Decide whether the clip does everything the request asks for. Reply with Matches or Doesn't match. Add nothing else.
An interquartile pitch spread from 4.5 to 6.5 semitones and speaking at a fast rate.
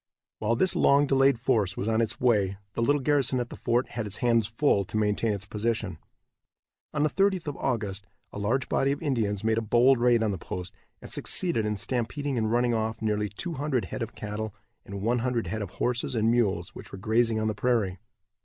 Doesn't match